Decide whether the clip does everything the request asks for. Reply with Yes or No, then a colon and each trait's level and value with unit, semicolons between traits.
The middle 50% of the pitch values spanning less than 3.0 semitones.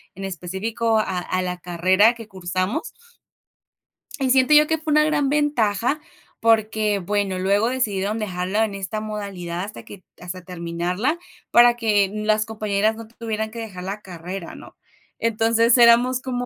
No: average, 3.6 semitones